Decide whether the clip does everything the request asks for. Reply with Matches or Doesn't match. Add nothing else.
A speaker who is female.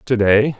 Doesn't match